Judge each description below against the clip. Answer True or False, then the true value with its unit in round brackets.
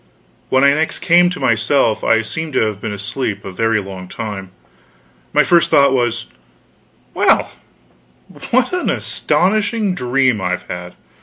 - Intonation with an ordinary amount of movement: False (7.7 semitones)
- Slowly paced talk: False (145 wpm)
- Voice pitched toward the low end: True (120 Hz)